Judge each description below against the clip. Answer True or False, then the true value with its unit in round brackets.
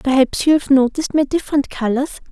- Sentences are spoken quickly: False (155 wpm)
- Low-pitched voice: False (275 Hz)